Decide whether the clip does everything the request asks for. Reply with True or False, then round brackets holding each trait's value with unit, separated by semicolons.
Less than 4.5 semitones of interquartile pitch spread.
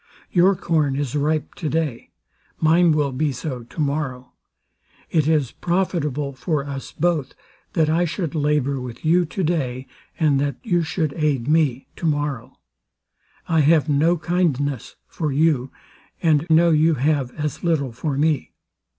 True (2.8 semitones)